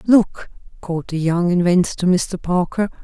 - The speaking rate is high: No, average, 160 wpm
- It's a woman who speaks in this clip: Yes, female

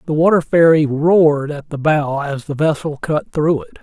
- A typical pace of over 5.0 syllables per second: No, 4.8 syllables/s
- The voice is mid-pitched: Yes, medium, 150 Hz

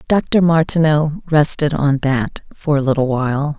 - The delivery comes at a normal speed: Yes, average, 150 wpm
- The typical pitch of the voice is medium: Yes, medium, 150 Hz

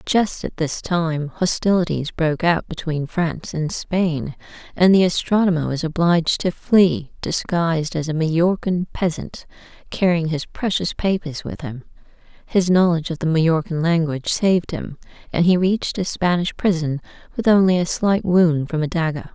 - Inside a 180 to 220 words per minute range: No, average, 160 wpm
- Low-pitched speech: No, medium, 170 Hz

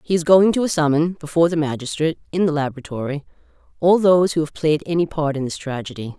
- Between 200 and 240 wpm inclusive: Yes, fast, 205 wpm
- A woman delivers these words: Yes, female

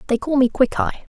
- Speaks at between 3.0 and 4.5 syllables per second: No, 5.6 syllables/s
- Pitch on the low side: No, very high, 265 Hz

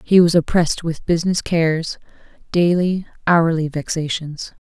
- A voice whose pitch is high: No, medium, 165 Hz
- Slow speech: Yes, slow, 115 wpm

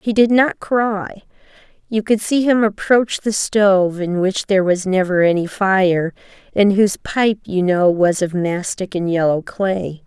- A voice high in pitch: Yes, high, 195 Hz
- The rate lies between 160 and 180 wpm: Yes, average, 175 wpm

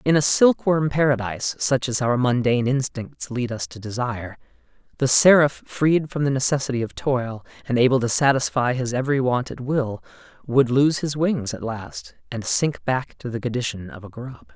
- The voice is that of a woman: No, male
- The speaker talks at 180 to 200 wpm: Yes, average, 185 wpm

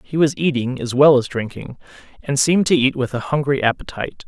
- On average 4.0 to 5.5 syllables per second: No, 5.9 syllables/s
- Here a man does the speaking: Yes, male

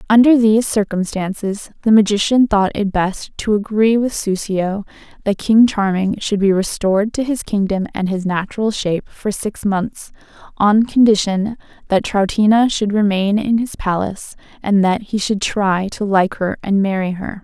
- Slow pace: No, average, 165 wpm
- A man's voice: No, female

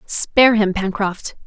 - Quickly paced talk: No, slow, 125 wpm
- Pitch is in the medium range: No, high, 210 Hz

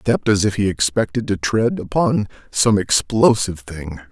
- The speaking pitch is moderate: No, low, 105 Hz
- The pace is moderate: Yes, average, 175 wpm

